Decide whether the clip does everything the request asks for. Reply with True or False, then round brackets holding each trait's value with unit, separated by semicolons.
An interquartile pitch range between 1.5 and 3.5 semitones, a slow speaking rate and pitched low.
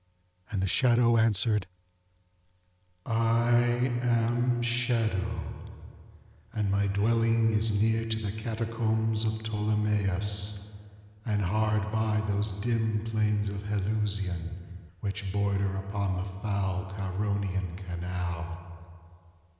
True (2.4 semitones; 100 wpm; 105 Hz)